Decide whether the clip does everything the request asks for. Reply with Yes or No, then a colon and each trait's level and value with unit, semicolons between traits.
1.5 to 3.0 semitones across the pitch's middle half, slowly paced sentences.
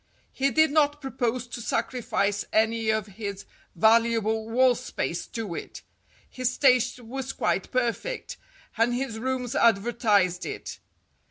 Yes: average, 2.7 semitones; slow, 125 wpm